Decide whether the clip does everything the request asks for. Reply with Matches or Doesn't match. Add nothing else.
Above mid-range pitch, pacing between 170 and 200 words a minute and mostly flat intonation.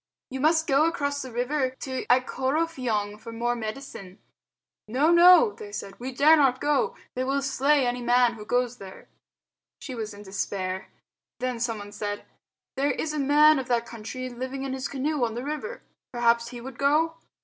Doesn't match